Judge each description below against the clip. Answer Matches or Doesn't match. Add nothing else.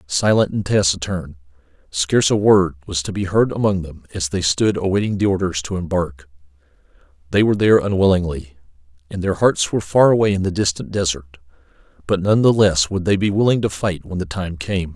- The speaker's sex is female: Doesn't match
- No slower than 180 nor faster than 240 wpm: Matches